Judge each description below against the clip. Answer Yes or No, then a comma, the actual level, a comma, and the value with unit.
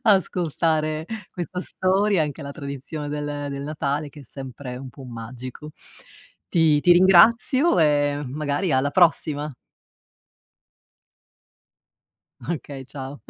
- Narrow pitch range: No, average, 3.6 semitones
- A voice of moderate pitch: Yes, medium, 150 Hz